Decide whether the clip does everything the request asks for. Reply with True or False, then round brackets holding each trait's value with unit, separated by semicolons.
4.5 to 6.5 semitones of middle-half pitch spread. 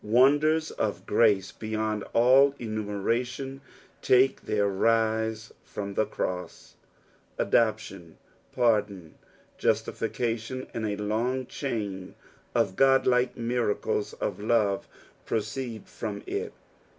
False (3.3 semitones)